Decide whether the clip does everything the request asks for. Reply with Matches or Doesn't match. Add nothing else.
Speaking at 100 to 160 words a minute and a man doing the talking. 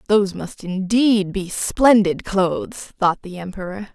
Doesn't match